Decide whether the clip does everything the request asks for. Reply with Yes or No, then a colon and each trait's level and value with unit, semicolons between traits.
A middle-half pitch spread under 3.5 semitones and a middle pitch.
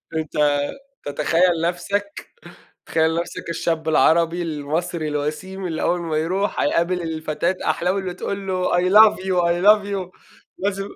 Yes: average, 2.8 semitones; medium, 175 Hz